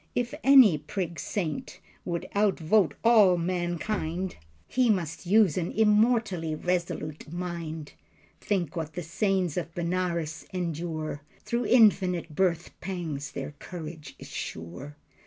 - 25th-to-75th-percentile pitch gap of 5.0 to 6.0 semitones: No, average, 3.5 semitones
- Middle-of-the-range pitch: Yes, medium, 175 Hz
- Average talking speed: No, slow, 115 wpm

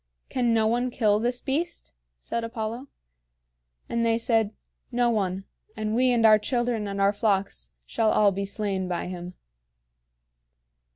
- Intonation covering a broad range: No, average, 3.1 semitones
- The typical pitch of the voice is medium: No, high, 220 Hz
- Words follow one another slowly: No, average, 150 wpm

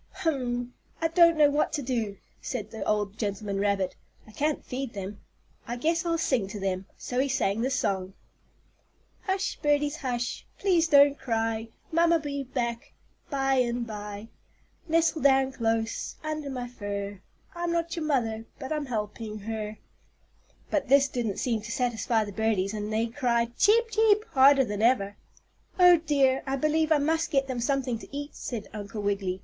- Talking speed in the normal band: Yes, average, 170 wpm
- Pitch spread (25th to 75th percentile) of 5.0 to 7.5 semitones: Yes, average, 5.3 semitones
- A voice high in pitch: Yes, very high, 250 Hz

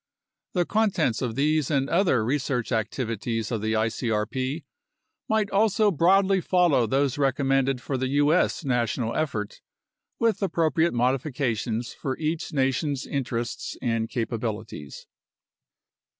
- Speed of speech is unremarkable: No, slow, 115 wpm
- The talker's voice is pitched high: No, low, 135 Hz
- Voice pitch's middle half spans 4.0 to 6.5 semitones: Yes, average, 5.3 semitones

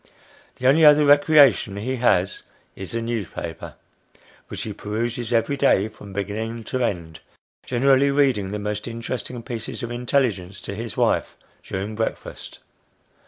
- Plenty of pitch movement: No, average, 4.1 semitones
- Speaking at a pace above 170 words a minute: No, average, 140 wpm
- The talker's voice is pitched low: Yes, low, 115 Hz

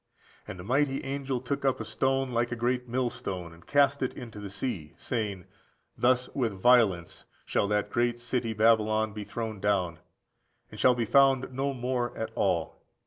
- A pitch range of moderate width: Yes, average, 3.9 semitones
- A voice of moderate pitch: No, low, 120 Hz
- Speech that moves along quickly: No, average, 175 wpm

